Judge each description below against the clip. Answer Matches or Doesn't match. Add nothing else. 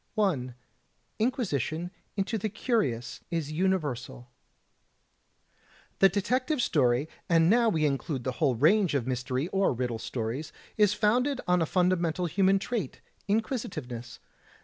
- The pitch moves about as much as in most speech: Doesn't match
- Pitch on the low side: Doesn't match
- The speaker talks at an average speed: Doesn't match